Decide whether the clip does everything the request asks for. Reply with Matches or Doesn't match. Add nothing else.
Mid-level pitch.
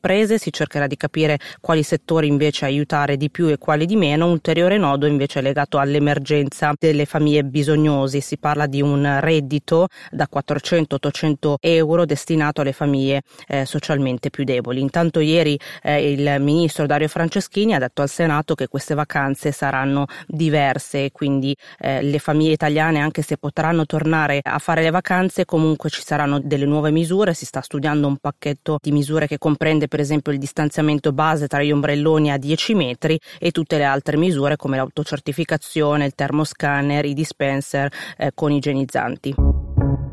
Matches